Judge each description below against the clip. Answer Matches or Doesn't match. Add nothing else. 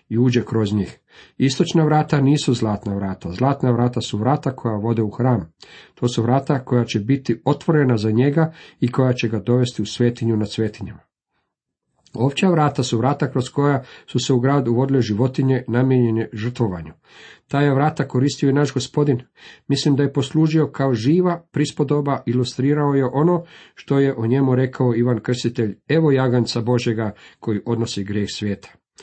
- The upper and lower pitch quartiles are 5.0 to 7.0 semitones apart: Doesn't match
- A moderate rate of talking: Doesn't match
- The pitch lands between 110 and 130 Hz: Matches